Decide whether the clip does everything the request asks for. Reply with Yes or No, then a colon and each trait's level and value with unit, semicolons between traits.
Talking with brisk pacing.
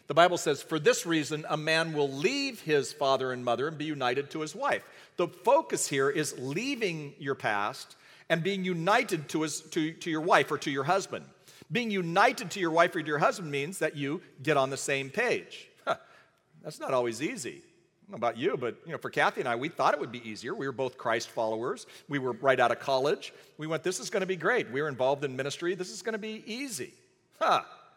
Yes: fast, 240 wpm